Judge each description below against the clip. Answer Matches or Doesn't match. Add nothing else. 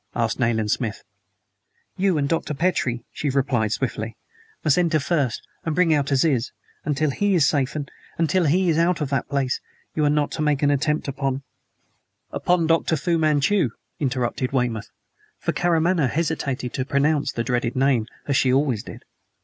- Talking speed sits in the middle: Matches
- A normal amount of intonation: Matches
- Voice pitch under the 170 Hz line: Matches